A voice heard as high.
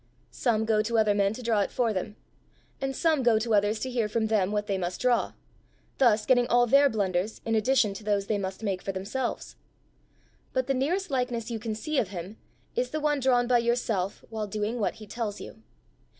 Yes: high, 225 Hz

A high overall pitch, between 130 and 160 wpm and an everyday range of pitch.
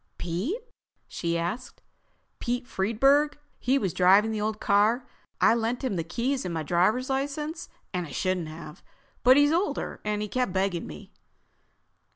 No: high, 215 Hz; average, 150 wpm; wide, 6.3 semitones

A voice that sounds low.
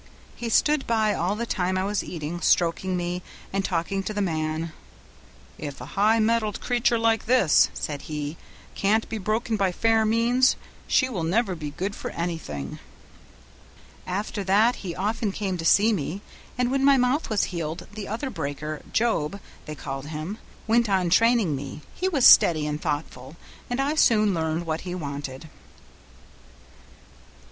No: high, 190 Hz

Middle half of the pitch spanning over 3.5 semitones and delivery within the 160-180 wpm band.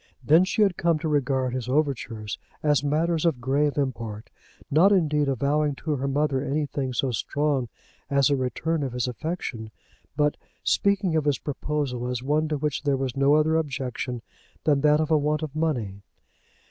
No: average, 2.9 semitones; average, 175 wpm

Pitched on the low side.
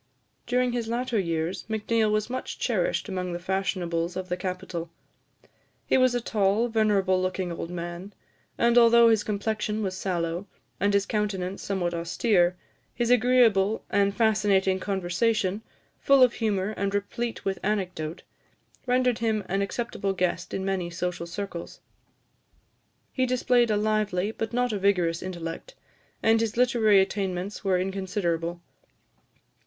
No: high, 200 Hz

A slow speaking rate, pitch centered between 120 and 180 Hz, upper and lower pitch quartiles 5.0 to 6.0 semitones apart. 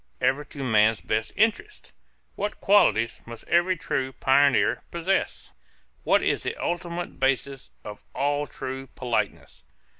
Yes: slow, 125 wpm; medium, 140 Hz; average, 5.3 semitones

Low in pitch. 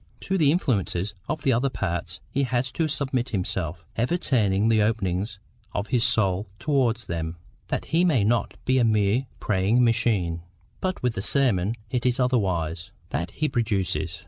Yes: low, 115 Hz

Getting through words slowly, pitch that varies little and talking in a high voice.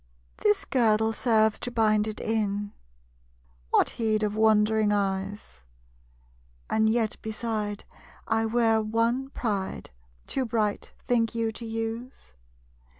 Yes: slow, 115 wpm; narrow, 1.4 semitones; high, 220 Hz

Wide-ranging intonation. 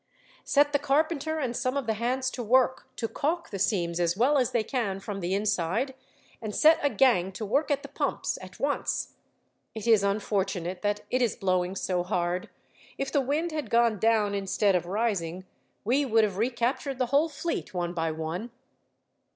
Yes: wide, 5.8 semitones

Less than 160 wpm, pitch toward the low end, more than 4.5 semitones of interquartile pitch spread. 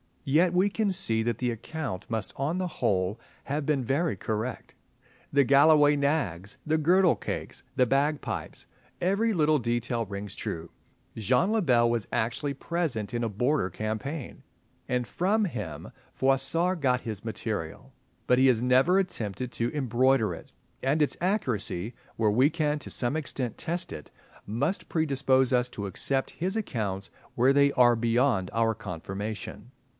Yes: average, 150 wpm; low, 130 Hz; wide, 5.4 semitones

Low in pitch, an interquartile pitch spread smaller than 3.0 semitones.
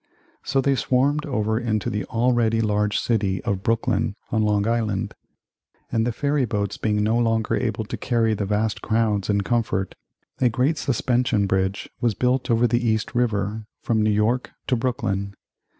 Yes: low, 110 Hz; narrow, 2.6 semitones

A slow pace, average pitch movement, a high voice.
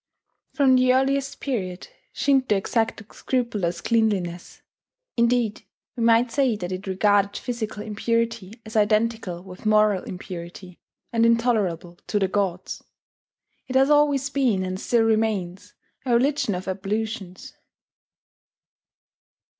Yes: slow, 115 wpm; average, 4.1 semitones; high, 215 Hz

